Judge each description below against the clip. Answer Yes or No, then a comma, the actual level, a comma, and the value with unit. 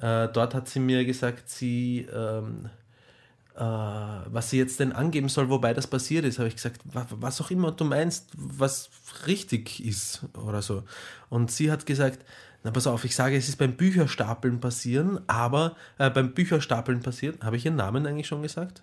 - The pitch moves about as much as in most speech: Yes, average, 3.6 semitones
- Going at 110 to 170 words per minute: No, average, 180 wpm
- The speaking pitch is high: No, low, 130 Hz